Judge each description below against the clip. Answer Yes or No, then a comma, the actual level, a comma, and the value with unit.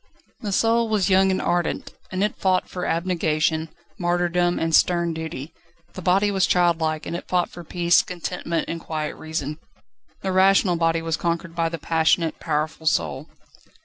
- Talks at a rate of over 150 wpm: Yes, average, 165 wpm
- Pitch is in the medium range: Yes, medium, 170 Hz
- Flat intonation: Yes, narrow, 2.3 semitones